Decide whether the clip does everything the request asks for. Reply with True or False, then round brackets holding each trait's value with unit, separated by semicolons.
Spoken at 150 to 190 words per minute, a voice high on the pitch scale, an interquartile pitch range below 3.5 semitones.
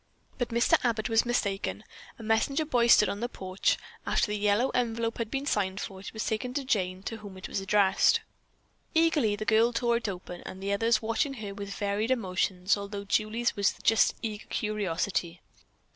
True (185 wpm; 215 Hz; 2.9 semitones)